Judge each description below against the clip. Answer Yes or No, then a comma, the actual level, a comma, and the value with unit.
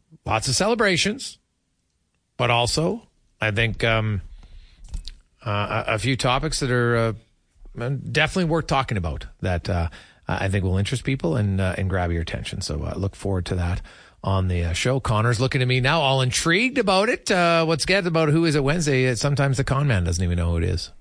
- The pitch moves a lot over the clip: Yes, wide, 7.6 semitones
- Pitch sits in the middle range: No, low, 115 Hz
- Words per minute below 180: No, average, 195 wpm